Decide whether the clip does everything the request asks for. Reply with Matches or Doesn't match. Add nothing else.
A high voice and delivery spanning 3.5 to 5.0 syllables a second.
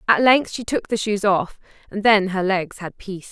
Matches